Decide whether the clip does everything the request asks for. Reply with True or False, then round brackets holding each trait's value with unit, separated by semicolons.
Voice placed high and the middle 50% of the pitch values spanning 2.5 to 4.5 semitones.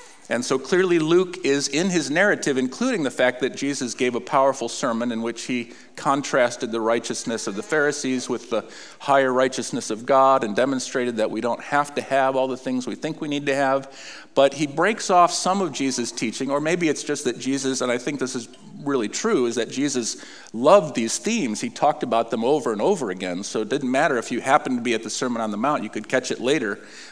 False (135 Hz; 3.4 semitones)